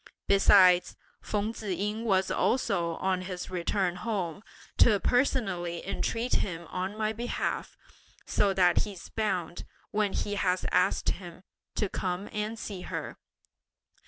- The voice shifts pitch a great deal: No, average, 2.8 semitones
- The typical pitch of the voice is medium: No, high, 195 Hz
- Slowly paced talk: Yes, slow, 130 wpm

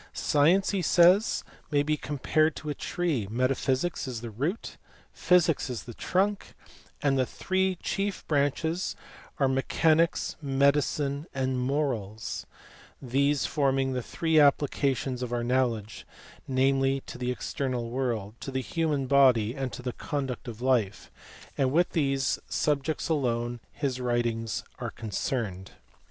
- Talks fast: No, average, 145 wpm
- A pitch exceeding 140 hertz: No, low, 135 Hz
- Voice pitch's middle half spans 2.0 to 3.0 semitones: No, average, 3.4 semitones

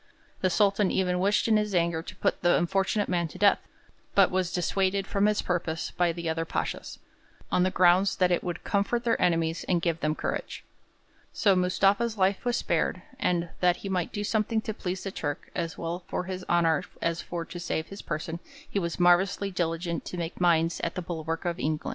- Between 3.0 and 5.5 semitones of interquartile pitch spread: No, narrow, 2.6 semitones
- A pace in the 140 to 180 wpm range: No, fast, 205 wpm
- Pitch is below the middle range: No, medium, 180 Hz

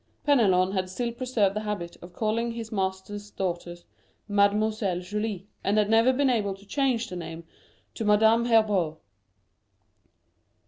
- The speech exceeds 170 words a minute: No, average, 140 wpm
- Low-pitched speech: No, high, 210 Hz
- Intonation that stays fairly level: No, average, 3.1 semitones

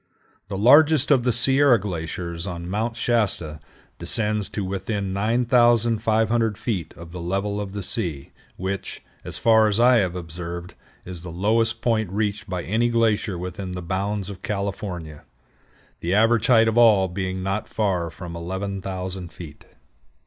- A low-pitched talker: Yes, low, 100 Hz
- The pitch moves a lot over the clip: No, average, 3.8 semitones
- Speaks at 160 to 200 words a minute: No, average, 150 wpm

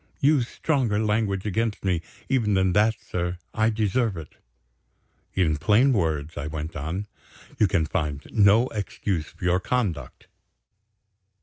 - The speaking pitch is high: No, low, 100 Hz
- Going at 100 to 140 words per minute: Yes, slow, 135 wpm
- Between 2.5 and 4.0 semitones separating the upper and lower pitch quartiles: No, average, 4.9 semitones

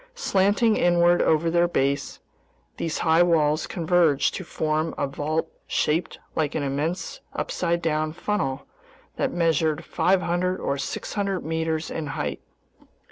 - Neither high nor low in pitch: Yes, medium, 165 Hz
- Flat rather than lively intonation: Yes, narrow, 2.3 semitones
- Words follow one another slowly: Yes, slow, 130 wpm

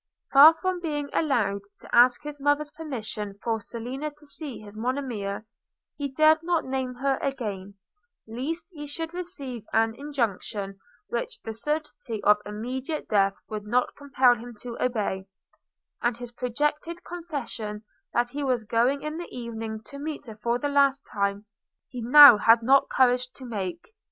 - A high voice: Yes, very high, 250 Hz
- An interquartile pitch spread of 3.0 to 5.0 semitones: Yes, average, 4.6 semitones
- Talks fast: No, average, 160 wpm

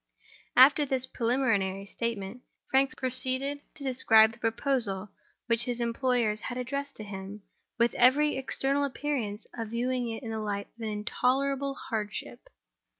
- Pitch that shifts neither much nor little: Yes, average, 3.5 semitones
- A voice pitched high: Yes, high, 245 Hz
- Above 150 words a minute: No, average, 145 wpm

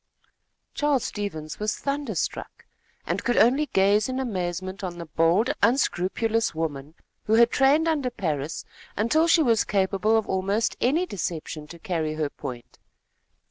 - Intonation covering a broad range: Yes, wide, 6.6 semitones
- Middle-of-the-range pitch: No, high, 205 Hz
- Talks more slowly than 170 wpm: Yes, average, 140 wpm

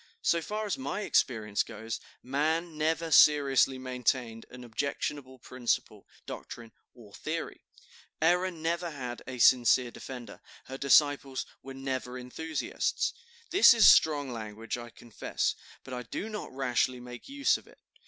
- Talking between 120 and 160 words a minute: Yes, average, 140 wpm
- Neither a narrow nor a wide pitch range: Yes, average, 4.4 semitones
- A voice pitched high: No, low, 130 Hz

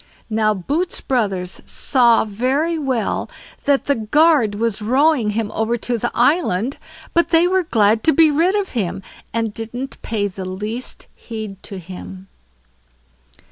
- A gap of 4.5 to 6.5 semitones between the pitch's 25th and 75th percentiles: Yes, wide, 5.5 semitones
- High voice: Yes, high, 230 Hz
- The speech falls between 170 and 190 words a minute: No, average, 145 wpm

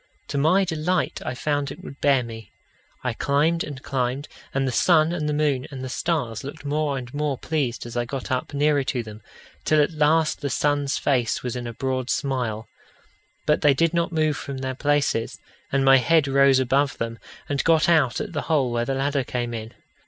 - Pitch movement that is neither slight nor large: Yes, average, 3.1 semitones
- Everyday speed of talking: No, fast, 210 wpm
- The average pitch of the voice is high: No, medium, 140 Hz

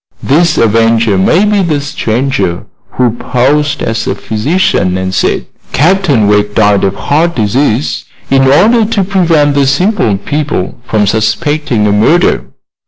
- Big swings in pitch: Yes, wide, 7.1 semitones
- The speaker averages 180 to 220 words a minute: No, average, 140 wpm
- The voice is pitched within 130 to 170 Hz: Yes, low, 135 Hz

